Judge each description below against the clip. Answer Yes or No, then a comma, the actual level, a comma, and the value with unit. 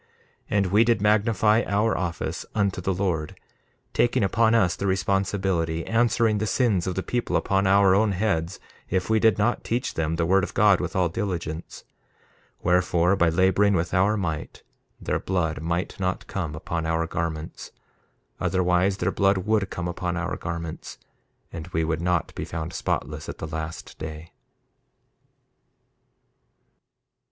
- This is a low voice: Yes, very low, 95 Hz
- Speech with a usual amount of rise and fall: Yes, average, 3.4 semitones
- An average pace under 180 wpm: Yes, average, 155 wpm